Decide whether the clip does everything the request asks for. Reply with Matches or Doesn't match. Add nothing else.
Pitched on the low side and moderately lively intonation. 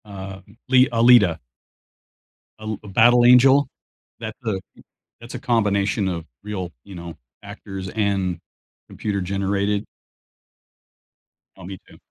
Matches